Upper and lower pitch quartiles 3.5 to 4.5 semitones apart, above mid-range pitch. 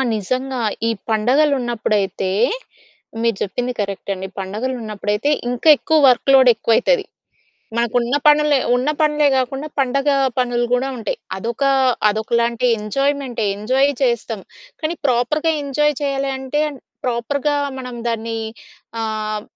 Yes: average, 3.8 semitones; high, 245 Hz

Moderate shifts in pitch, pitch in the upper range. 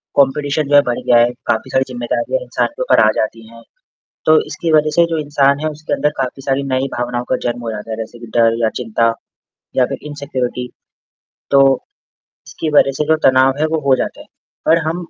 No: average, 3.9 semitones; low, 135 Hz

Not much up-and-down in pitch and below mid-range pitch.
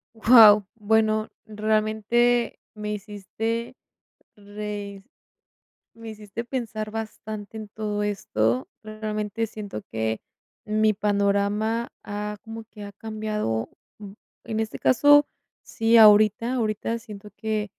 No: narrow, 1.3 semitones; high, 215 Hz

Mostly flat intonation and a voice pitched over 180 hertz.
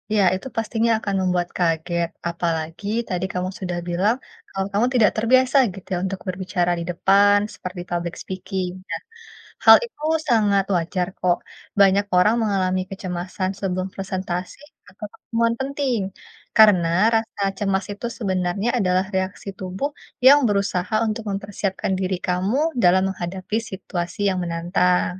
Yes: narrow, 2.3 semitones; high, 190 Hz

